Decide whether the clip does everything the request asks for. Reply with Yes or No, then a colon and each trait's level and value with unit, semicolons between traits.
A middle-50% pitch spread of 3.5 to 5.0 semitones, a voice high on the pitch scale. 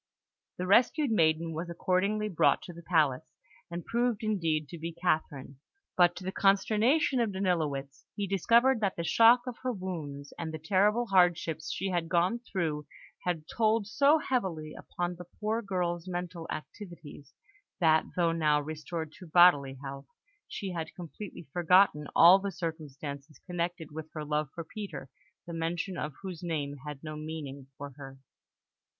No: average, 4.0 semitones; medium, 170 Hz